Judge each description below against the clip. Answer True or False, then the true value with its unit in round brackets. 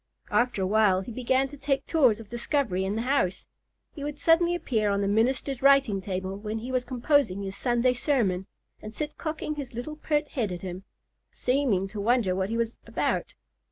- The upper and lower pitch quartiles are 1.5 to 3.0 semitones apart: False (5.6 semitones)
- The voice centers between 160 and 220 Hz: False (235 Hz)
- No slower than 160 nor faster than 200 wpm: True (195 wpm)